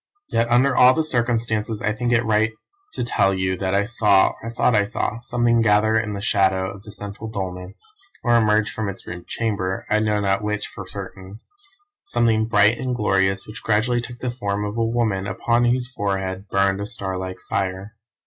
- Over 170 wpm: Yes, average, 195 wpm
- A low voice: Yes, low, 105 Hz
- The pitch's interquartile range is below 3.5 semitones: Yes, average, 3.1 semitones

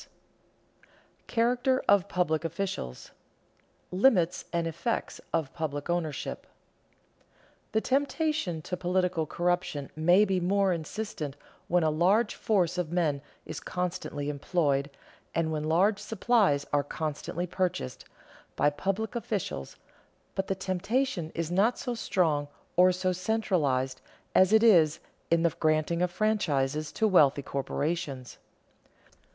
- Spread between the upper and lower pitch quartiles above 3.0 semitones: Yes, average, 4.2 semitones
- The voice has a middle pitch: Yes, medium, 175 Hz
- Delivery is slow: Yes, slow, 125 wpm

